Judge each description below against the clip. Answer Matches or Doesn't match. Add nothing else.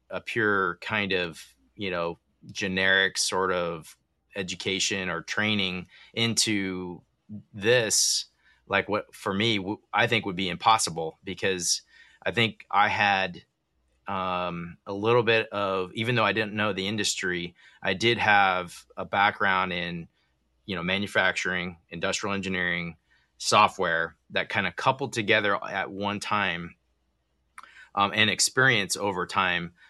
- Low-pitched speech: Matches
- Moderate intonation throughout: Matches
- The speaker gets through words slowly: Matches